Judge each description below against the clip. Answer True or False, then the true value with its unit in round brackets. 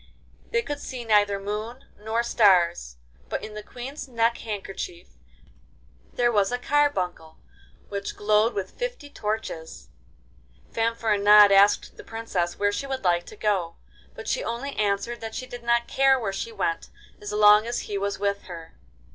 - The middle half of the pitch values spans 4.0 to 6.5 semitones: False (3.1 semitones)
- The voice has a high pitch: True (210 Hz)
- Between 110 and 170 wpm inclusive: True (160 wpm)